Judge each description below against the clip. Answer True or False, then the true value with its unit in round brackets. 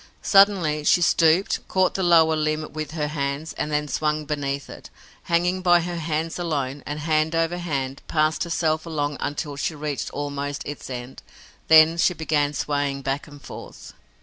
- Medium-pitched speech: True (155 Hz)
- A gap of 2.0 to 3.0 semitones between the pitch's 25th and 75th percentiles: True (2.4 semitones)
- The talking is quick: False (170 wpm)